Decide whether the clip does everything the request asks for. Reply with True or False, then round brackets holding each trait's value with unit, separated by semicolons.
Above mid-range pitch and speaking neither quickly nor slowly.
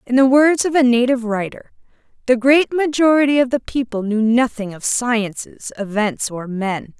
True (240 Hz; 170 wpm)